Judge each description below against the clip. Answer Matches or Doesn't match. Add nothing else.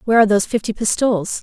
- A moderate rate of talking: Doesn't match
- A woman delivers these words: Matches